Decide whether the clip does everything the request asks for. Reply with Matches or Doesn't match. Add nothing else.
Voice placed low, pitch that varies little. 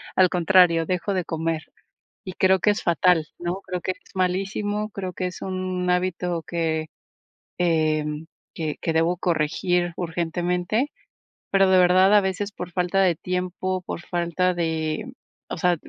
Doesn't match